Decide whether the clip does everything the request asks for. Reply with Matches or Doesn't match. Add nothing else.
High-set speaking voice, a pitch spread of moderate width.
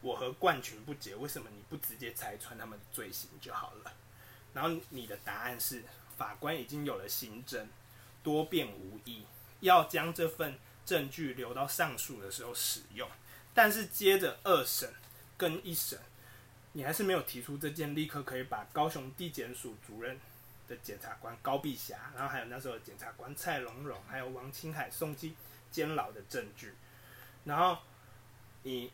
Doesn't match